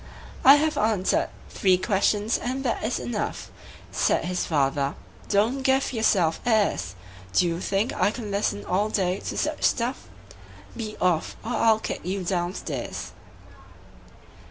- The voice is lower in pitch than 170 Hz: No, high, 205 Hz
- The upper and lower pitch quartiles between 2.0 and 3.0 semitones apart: No, average, 4.5 semitones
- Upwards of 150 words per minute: No, average, 145 wpm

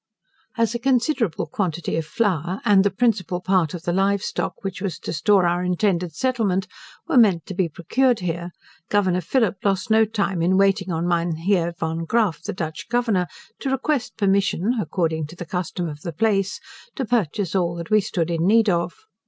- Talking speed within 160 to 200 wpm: Yes, average, 185 wpm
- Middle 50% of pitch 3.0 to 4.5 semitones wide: Yes, average, 3.8 semitones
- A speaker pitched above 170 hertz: Yes, medium, 185 Hz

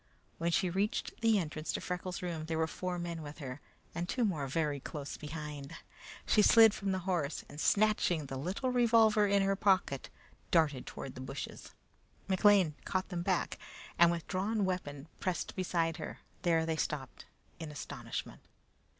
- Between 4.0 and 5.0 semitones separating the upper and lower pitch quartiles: Yes, average, 4.3 semitones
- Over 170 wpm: No, average, 165 wpm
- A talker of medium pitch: Yes, medium, 170 Hz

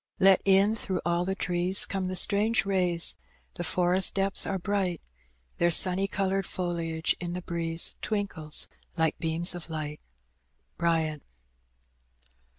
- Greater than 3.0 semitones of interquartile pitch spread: No, narrow, 2.5 semitones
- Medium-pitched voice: Yes, medium, 180 Hz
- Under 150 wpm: Yes, slow, 135 wpm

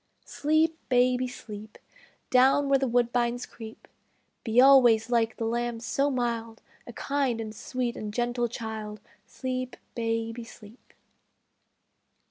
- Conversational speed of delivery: No, slow, 120 wpm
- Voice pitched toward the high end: Yes, high, 240 Hz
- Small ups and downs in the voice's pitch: Yes, narrow, 2.0 semitones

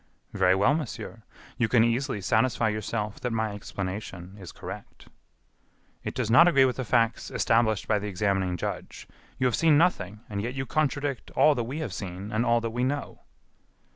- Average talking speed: Yes, average, 185 wpm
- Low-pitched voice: Yes, low, 115 Hz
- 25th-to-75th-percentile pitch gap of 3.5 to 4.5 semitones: Yes, average, 4.1 semitones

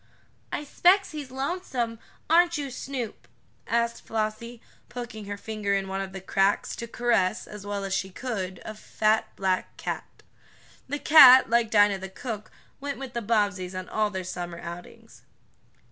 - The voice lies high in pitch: Yes, high, 215 Hz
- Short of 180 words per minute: Yes, average, 160 wpm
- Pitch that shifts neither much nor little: Yes, average, 4.4 semitones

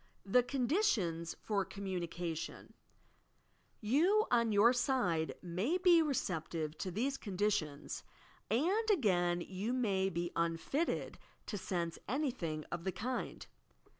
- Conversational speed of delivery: No, slow, 115 wpm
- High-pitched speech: Yes, high, 205 Hz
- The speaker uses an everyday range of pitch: No, wide, 7.0 semitones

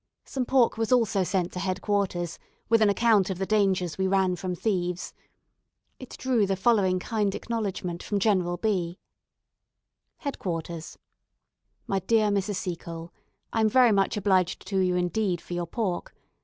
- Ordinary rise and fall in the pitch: Yes, average, 3.3 semitones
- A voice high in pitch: Yes, high, 195 Hz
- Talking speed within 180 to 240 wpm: No, average, 160 wpm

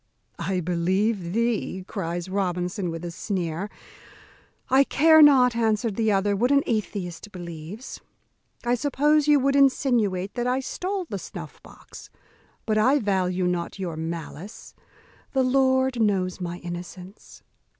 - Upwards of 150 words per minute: No, slow, 135 wpm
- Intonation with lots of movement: Yes, wide, 6.1 semitones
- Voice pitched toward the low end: No, high, 205 Hz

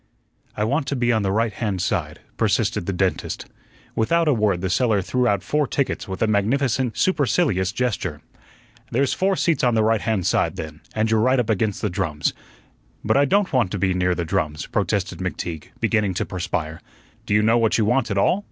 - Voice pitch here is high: No, low, 110 Hz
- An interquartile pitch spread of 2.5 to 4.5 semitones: No, average, 5.1 semitones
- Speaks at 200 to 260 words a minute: Yes, fast, 205 wpm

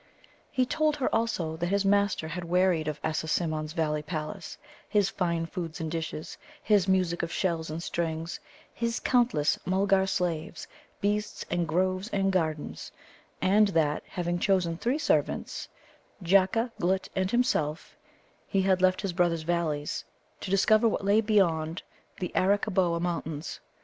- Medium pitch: Yes, medium, 180 Hz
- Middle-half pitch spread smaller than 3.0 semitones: No, average, 3.3 semitones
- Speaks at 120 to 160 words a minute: Yes, average, 145 wpm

